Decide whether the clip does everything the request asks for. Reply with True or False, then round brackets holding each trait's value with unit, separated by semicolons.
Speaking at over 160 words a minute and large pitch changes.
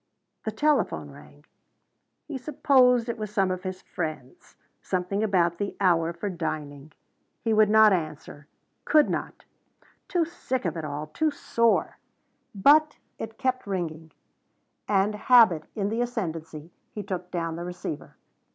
False (140 wpm; 5.8 semitones)